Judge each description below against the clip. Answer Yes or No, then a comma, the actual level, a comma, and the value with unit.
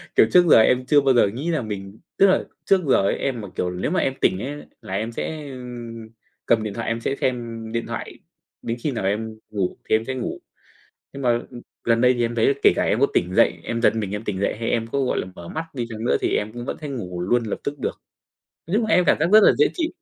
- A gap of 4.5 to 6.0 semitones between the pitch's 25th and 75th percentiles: No, average, 4.1 semitones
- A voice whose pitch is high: No, low, 120 Hz